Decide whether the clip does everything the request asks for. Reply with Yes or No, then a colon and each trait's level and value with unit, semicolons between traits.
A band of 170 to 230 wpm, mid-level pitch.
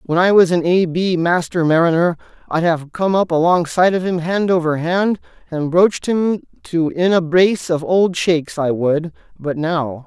Yes: average, 190 wpm; medium, 170 Hz